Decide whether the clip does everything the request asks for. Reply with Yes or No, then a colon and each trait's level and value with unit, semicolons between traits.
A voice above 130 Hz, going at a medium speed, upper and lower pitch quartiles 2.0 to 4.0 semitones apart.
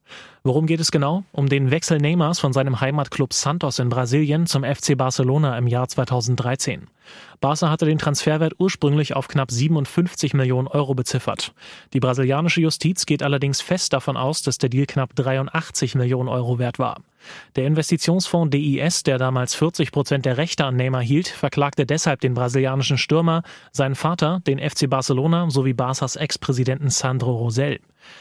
Yes: medium, 140 Hz; average, 160 wpm; average, 2.9 semitones